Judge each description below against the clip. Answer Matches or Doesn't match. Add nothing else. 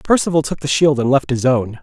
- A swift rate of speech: Matches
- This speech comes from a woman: Doesn't match